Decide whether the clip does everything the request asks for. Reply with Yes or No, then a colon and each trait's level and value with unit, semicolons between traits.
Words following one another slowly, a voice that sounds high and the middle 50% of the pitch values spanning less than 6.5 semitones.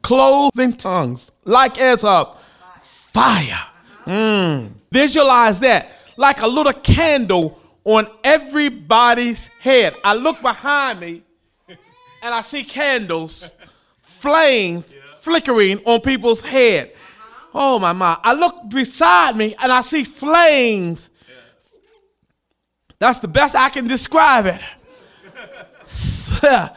Yes: slow, 105 wpm; very high, 250 Hz; average, 5.3 semitones